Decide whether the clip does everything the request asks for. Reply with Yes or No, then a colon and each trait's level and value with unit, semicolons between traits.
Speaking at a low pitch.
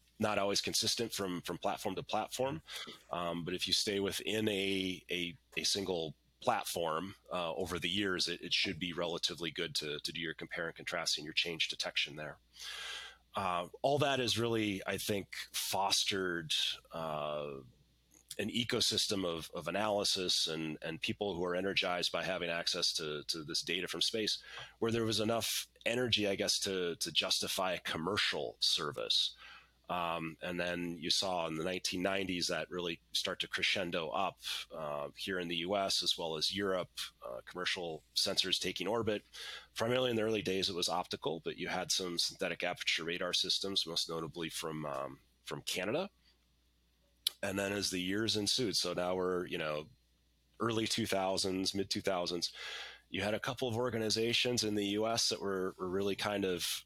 Yes: very low, 95 Hz